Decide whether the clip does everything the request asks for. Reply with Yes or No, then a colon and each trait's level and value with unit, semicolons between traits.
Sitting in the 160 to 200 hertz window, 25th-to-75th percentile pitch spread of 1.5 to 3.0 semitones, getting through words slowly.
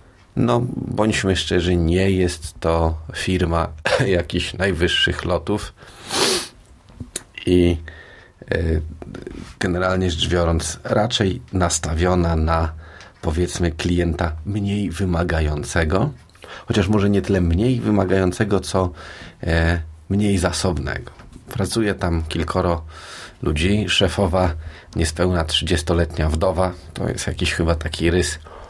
No: very low, 90 Hz; narrow, 2.5 semitones; slow, 95 wpm